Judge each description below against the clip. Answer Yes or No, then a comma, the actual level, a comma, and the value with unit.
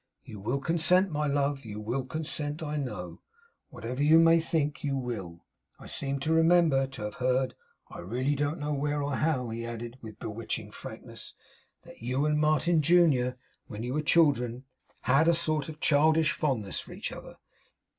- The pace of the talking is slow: No, average, 175 wpm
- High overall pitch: No, medium, 140 Hz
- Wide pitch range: No, average, 4.0 semitones